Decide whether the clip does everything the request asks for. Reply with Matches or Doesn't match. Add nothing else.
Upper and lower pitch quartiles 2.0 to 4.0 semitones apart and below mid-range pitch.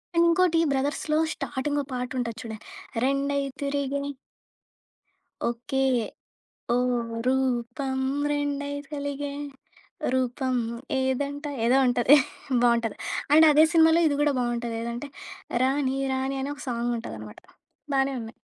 Doesn't match